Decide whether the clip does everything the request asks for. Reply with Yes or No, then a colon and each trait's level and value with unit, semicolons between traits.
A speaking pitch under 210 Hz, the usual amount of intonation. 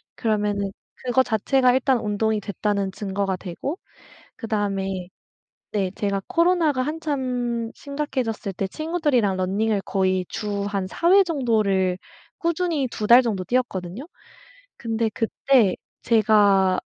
No: high, 220 Hz; average, 4.9 semitones